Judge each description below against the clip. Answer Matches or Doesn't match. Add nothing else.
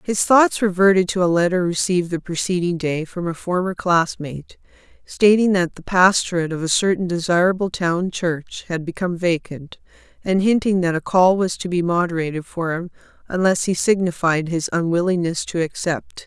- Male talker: Doesn't match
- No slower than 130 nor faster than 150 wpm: Doesn't match